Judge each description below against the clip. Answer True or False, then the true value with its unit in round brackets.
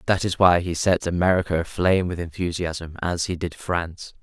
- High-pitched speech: False (90 Hz)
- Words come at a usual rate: True (185 wpm)